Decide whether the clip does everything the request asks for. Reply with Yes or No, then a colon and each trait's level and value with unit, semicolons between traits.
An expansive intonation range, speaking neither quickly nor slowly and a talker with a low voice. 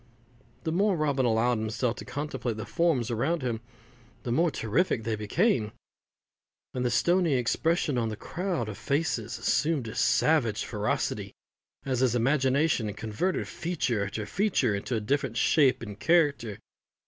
Yes: wide, 6.1 semitones; average, 150 wpm; low, 125 Hz